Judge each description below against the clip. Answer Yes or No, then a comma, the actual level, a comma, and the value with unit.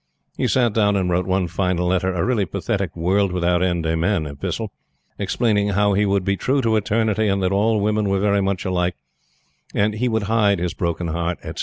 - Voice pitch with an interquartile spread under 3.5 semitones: Yes, average, 2.7 semitones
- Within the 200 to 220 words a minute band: Yes, fast, 205 wpm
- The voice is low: Yes, low, 100 Hz